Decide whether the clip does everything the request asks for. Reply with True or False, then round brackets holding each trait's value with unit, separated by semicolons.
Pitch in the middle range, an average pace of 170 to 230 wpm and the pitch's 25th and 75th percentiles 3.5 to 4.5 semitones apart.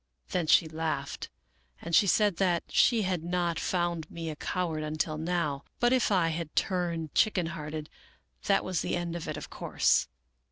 False (170 Hz; 175 wpm; 2.4 semitones)